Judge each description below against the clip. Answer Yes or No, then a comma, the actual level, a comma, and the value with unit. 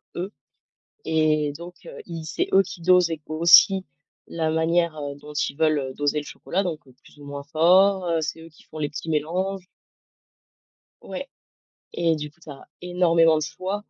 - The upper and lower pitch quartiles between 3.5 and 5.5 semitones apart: No, average, 2.7 semitones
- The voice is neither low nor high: Yes, medium, 160 Hz